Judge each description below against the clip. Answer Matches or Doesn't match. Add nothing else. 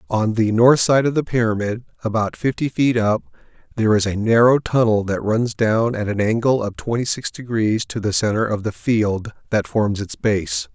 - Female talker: Doesn't match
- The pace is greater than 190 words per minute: Matches